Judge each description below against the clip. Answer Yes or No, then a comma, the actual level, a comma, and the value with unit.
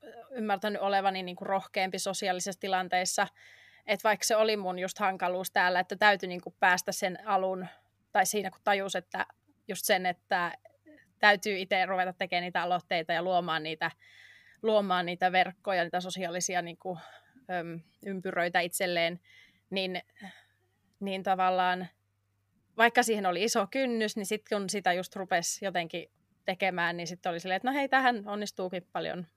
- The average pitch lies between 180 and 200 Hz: Yes, medium, 185 Hz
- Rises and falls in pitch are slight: Yes, narrow, 2.3 semitones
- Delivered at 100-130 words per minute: No, average, 150 wpm